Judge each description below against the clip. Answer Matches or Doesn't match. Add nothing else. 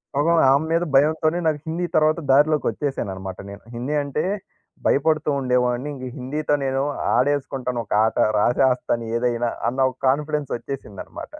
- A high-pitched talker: Doesn't match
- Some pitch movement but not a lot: Matches